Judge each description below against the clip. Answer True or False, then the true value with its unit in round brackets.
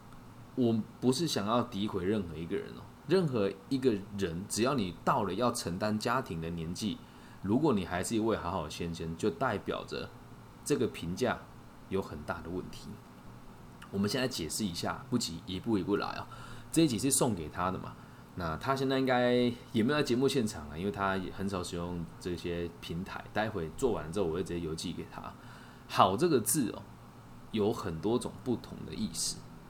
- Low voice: True (100 Hz)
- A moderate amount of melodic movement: False (6.0 semitones)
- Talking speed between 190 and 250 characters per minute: False (280 characters per minute)